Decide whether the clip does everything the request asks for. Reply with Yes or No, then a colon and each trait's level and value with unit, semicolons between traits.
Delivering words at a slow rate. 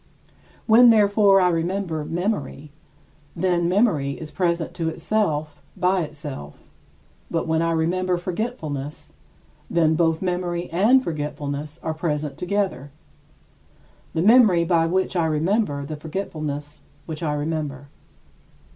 Yes: slow, 120 wpm